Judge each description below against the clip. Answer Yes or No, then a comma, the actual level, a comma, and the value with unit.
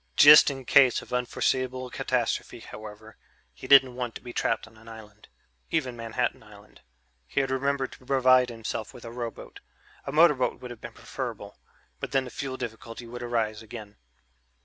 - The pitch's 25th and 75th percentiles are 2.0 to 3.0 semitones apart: Yes, narrow, 2.6 semitones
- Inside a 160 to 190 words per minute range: Yes, average, 170 wpm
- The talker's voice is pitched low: Yes, low, 125 Hz